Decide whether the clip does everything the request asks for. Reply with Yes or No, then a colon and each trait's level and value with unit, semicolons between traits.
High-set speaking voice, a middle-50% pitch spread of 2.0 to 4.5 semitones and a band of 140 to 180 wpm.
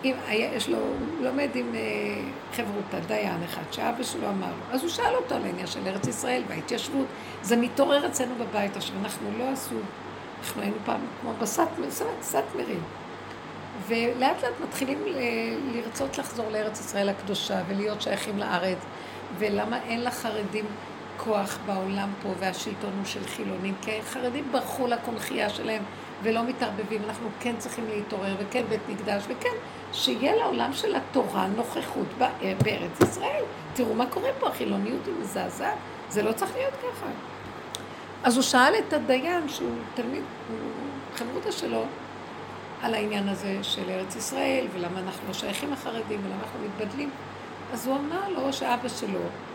Yes: high, 230 Hz; average, 3.8 semitones; fast, 150 wpm